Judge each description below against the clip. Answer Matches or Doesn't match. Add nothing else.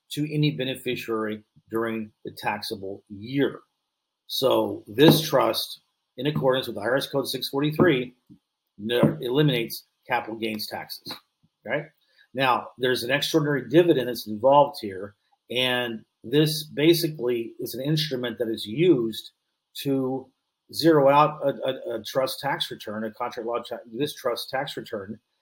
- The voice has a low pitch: Matches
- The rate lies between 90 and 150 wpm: Matches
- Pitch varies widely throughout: Doesn't match